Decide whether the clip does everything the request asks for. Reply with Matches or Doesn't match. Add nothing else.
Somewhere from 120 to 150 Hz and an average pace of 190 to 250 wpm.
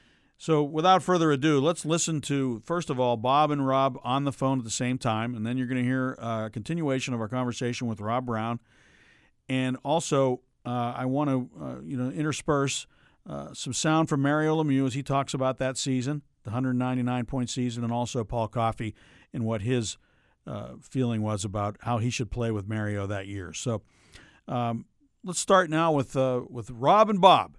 Matches